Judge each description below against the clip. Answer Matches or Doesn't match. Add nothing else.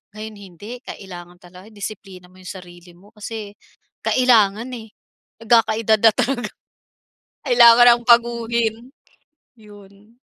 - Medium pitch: Doesn't match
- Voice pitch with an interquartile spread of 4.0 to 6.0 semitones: Doesn't match